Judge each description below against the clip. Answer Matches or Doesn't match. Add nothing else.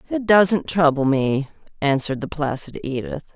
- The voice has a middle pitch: Matches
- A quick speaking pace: Doesn't match